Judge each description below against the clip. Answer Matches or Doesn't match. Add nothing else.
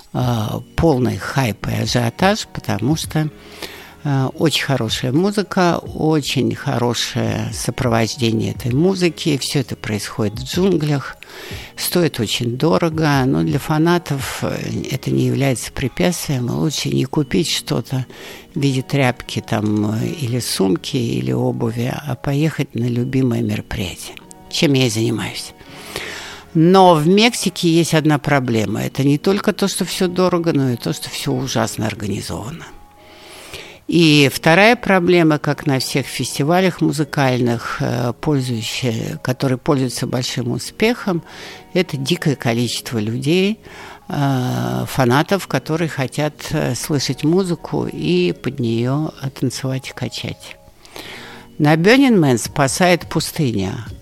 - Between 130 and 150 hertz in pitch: Matches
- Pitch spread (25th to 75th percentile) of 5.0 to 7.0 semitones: Matches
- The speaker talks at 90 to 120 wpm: Matches